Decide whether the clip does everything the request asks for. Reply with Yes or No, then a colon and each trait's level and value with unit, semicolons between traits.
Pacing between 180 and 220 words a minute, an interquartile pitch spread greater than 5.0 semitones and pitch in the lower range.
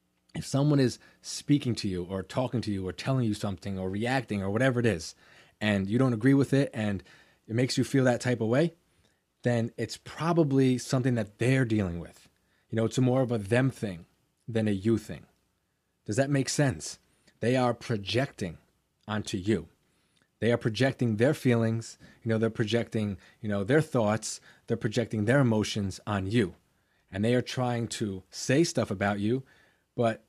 No: average, 185 wpm; average, 3.6 semitones; low, 115 Hz